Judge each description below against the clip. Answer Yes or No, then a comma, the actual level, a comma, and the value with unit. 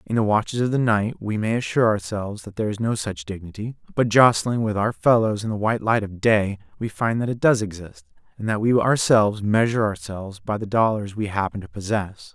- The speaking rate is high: Yes, fast, 225 wpm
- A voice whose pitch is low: Yes, low, 110 Hz